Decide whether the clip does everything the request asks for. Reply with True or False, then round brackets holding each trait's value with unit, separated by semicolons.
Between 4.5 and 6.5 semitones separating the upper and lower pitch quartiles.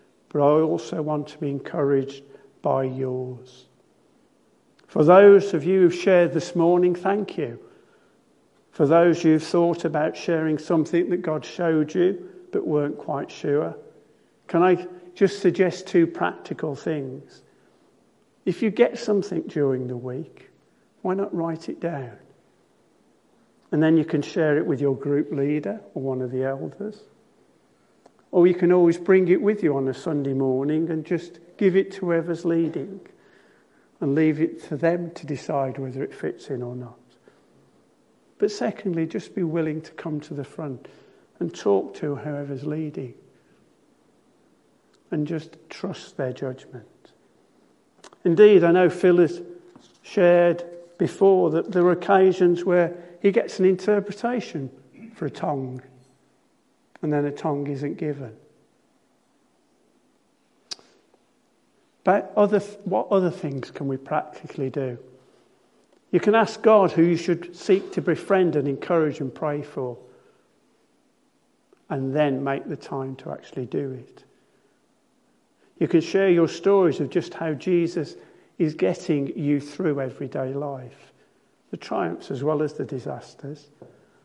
False (4.0 semitones)